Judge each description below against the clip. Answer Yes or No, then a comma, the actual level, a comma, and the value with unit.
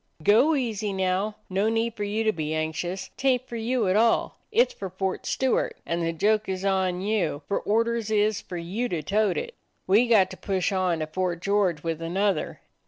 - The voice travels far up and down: No, average, 3.5 semitones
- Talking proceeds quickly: Yes, fast, 210 wpm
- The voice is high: Yes, high, 200 Hz